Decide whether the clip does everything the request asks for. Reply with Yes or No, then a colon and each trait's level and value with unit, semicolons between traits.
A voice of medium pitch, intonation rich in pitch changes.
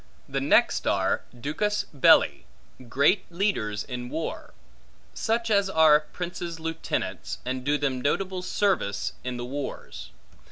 Yes: medium, 155 Hz; wide, 6.5 semitones